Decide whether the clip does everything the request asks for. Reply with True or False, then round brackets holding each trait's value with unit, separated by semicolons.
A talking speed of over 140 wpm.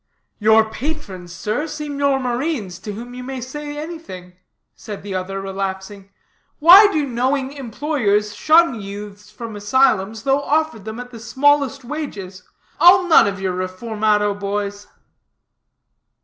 False (135 wpm)